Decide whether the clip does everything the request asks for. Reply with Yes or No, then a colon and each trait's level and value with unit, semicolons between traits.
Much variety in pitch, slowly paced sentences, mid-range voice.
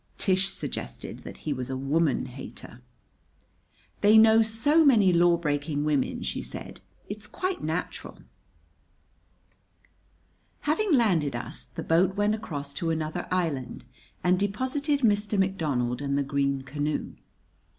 Yes: wide, 6.9 semitones; slow, 125 wpm; medium, 175 Hz